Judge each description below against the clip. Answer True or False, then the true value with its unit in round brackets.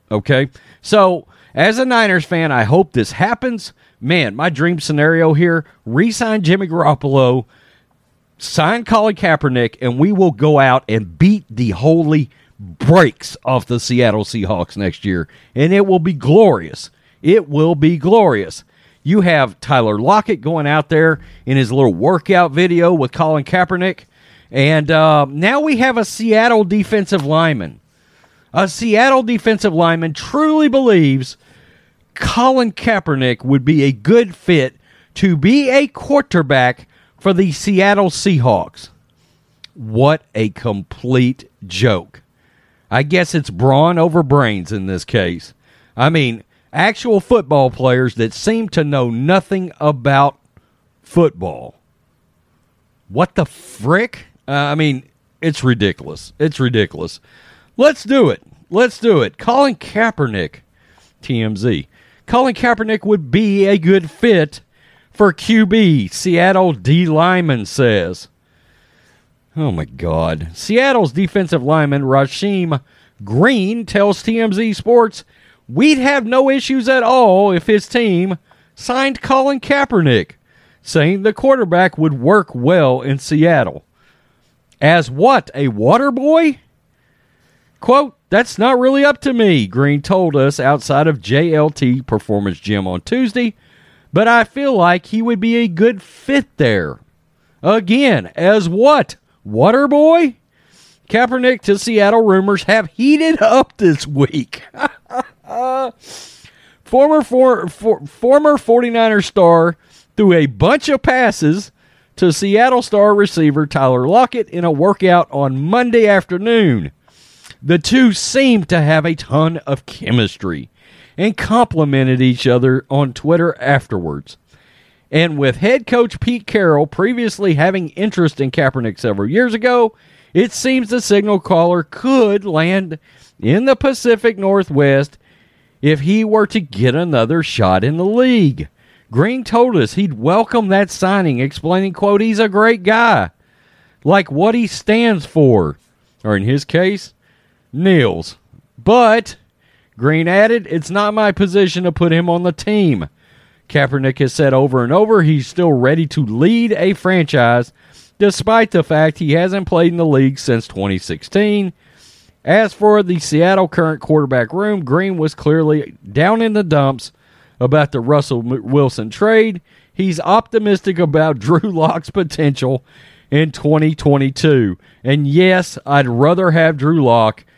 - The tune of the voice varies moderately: False (7.4 semitones)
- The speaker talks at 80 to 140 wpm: True (135 wpm)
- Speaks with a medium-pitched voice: True (170 Hz)